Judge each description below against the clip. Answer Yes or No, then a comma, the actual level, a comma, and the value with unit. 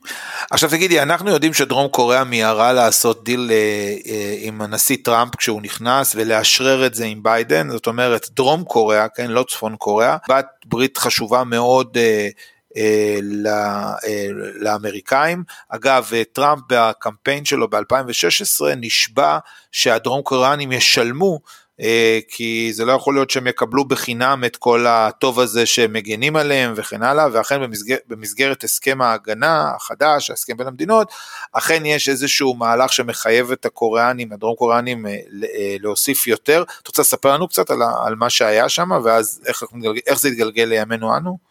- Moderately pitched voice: No, low, 120 Hz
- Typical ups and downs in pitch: Yes, average, 3.3 semitones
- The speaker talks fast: No, average, 135 wpm